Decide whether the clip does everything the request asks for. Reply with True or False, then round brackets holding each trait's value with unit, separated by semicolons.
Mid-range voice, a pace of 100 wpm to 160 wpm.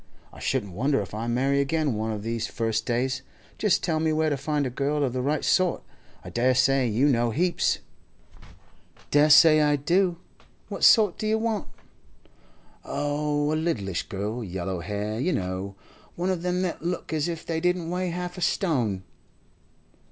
False (145 Hz; 170 wpm)